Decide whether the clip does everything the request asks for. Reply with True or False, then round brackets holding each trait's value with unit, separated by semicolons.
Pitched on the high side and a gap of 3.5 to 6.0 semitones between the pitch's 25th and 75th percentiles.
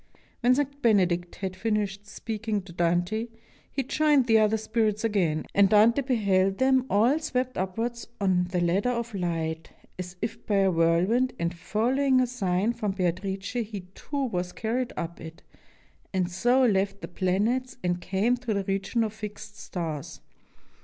True (205 Hz; 4.6 semitones)